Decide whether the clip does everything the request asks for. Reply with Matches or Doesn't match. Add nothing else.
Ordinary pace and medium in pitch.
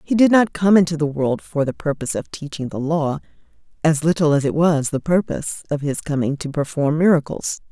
Doesn't match